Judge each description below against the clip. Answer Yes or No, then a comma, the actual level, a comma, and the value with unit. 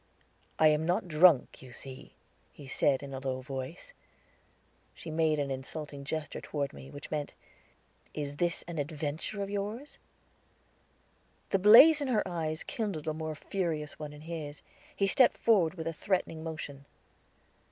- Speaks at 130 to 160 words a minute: Yes, average, 155 wpm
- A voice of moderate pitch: Yes, medium, 155 Hz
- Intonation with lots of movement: No, average, 3.7 semitones